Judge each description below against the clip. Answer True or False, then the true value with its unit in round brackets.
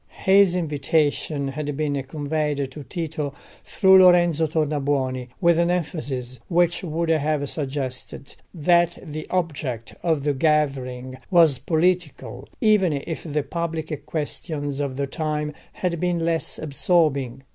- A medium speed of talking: False (125 wpm)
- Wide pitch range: False (3.3 semitones)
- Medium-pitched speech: True (150 Hz)